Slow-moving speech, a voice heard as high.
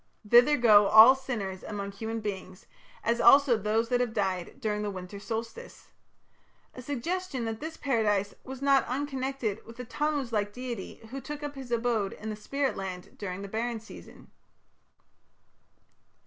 No: average, 160 wpm; high, 230 Hz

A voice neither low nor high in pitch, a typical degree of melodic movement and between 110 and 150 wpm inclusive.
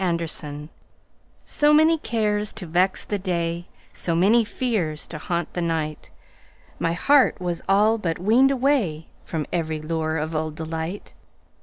Yes: medium, 175 Hz; average, 5.0 semitones; slow, 135 wpm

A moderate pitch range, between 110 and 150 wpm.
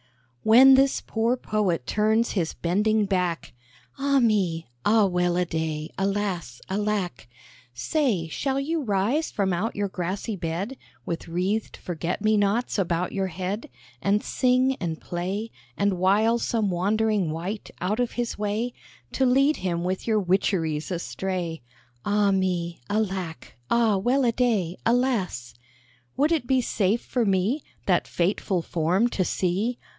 Yes: average, 4.2 semitones; average, 145 wpm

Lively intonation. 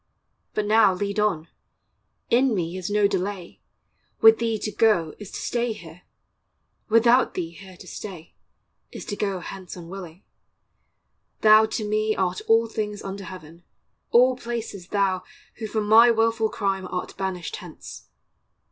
No: average, 3.2 semitones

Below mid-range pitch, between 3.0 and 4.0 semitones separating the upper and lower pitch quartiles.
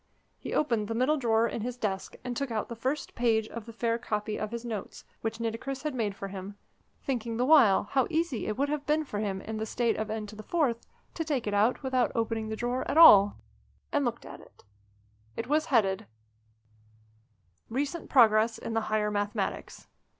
No: high, 230 Hz; average, 3.3 semitones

